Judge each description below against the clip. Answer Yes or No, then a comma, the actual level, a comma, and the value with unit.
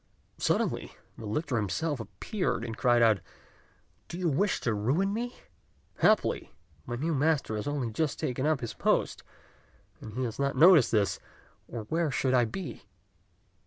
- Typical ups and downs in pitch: No, wide, 6.0 semitones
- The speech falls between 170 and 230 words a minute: No, average, 160 wpm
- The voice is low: Yes, low, 130 Hz